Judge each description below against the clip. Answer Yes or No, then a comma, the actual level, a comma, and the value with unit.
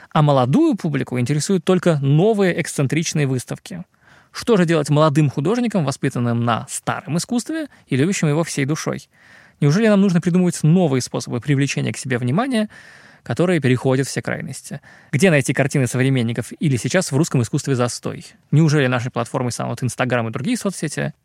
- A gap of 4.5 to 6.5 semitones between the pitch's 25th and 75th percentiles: Yes, average, 5.3 semitones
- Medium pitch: Yes, medium, 150 Hz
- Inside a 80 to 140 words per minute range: No, average, 155 wpm